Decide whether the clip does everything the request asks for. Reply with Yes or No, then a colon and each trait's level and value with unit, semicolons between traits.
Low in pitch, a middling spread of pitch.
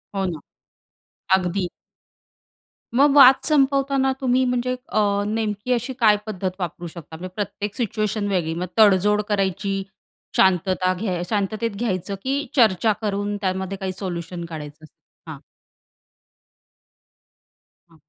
No: high, 200 Hz; average, 3.7 semitones